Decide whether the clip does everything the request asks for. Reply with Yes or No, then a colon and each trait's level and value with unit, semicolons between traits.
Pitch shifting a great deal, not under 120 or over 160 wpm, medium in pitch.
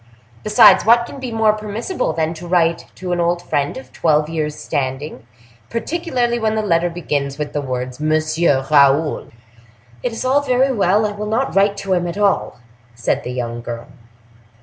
No: wide, 6.6 semitones; average, 175 wpm; medium, 175 Hz